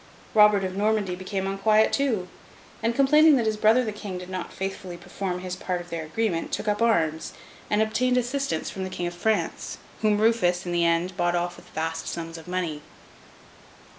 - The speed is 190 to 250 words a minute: Yes, average, 195 wpm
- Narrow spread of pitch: No, average, 3.9 semitones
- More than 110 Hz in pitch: Yes, high, 190 Hz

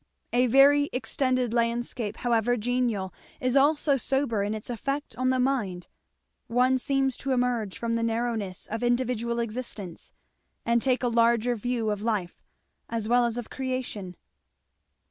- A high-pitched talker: Yes, high, 240 Hz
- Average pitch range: No, narrow, 2.3 semitones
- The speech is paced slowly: No, average, 145 wpm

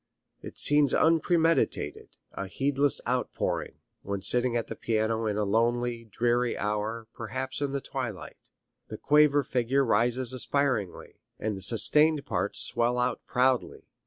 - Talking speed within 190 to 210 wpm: No, slow, 135 wpm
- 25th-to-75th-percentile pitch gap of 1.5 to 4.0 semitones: Yes, average, 3.6 semitones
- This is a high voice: No, low, 120 Hz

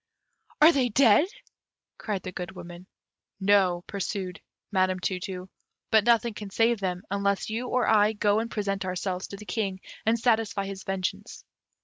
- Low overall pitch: No, high, 200 Hz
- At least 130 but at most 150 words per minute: No, average, 160 wpm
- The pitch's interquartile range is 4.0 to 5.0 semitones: No, average, 2.8 semitones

